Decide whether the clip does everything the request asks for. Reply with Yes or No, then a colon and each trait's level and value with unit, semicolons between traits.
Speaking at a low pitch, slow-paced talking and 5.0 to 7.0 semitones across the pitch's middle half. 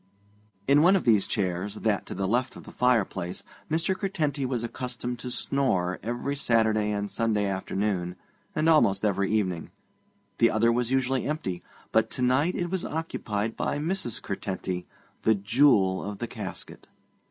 No: low, 115 Hz; average, 160 wpm; average, 5.3 semitones